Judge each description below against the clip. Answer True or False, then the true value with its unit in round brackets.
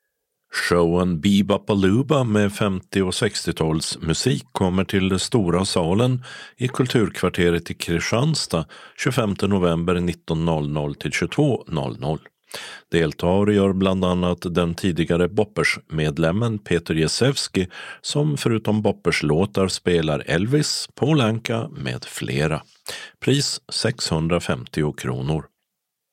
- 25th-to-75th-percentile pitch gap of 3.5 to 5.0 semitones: True (4.2 semitones)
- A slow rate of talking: True (95 wpm)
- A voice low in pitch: True (90 Hz)